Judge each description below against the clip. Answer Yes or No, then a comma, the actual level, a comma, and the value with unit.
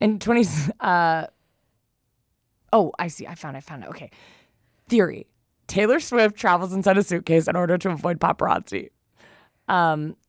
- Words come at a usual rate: Yes, average, 150 wpm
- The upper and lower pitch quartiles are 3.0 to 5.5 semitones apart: Yes, average, 4.1 semitones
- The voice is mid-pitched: Yes, medium, 170 Hz